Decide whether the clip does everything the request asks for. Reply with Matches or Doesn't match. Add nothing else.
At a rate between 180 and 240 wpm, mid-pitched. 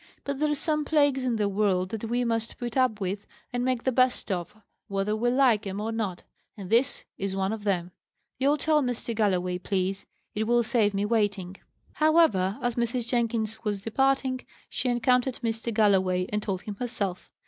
Doesn't match